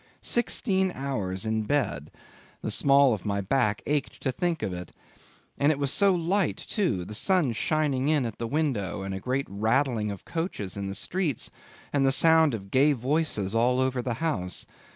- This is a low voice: Yes, low, 130 Hz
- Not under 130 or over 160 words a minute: No, average, 185 wpm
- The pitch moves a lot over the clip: Yes, wide, 6.7 semitones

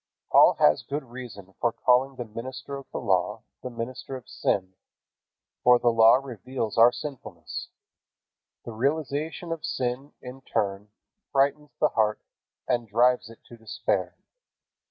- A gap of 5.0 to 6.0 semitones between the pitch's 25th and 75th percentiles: No, average, 2.9 semitones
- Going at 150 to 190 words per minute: No, average, 140 wpm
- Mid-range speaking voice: No, low, 125 Hz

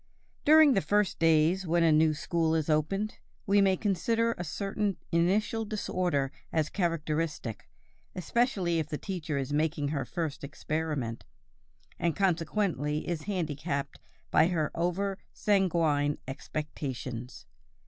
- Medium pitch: Yes, medium, 165 Hz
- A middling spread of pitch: Yes, average, 4.4 semitones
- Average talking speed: No, slow, 125 wpm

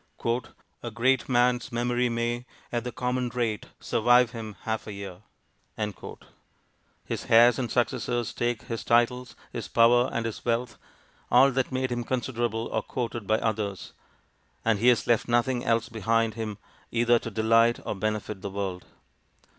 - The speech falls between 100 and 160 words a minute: Yes, average, 155 wpm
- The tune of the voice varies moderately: No, narrow, 1.6 semitones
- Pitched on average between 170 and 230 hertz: No, low, 115 Hz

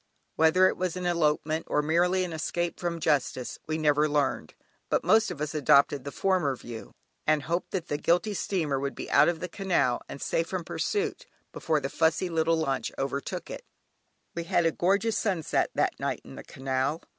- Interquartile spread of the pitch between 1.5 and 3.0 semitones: No, average, 3.4 semitones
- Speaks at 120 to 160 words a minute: No, average, 190 wpm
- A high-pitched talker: No, medium, 160 Hz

